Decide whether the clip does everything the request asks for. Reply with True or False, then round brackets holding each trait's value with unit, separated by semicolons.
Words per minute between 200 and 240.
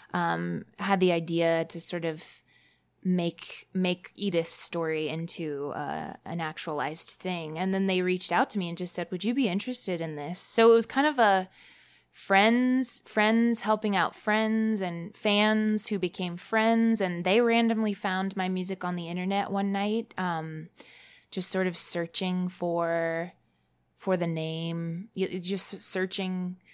False (155 wpm)